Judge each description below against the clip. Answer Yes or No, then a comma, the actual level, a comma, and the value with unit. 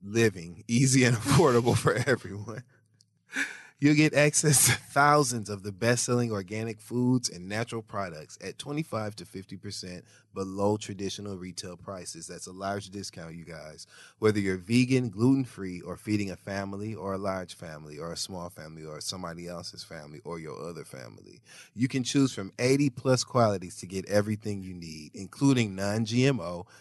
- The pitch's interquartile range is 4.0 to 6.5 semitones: Yes, average, 4.7 semitones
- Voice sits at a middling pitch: No, low, 105 Hz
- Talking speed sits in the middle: Yes, average, 165 wpm